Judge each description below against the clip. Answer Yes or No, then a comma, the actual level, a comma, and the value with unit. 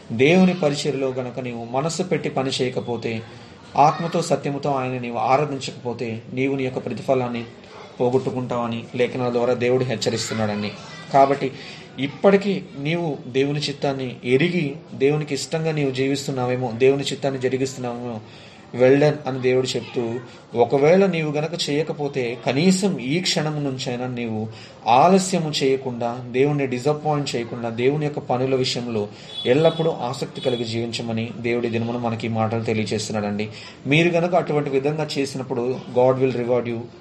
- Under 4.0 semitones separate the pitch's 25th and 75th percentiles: Yes, average, 3.5 semitones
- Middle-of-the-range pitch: No, low, 130 Hz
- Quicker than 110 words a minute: Yes, average, 120 wpm